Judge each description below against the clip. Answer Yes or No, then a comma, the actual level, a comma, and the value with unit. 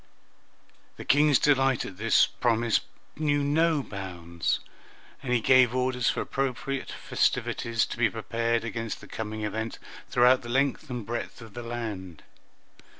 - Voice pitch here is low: Yes, low, 120 Hz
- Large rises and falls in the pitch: No, average, 3.0 semitones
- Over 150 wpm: No, average, 145 wpm